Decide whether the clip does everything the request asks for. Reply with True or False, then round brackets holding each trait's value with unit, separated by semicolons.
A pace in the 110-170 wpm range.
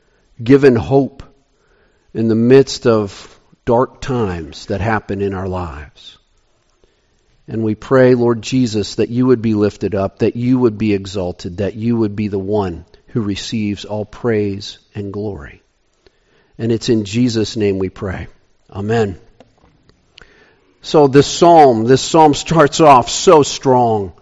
True (145 wpm)